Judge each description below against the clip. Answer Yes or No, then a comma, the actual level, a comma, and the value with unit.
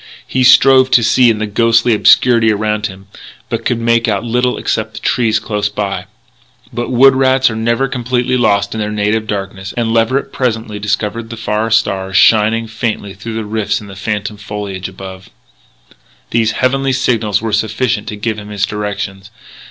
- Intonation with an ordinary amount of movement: No, narrow, 2.3 semitones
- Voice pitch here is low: Yes, low, 110 Hz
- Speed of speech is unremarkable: Yes, average, 175 wpm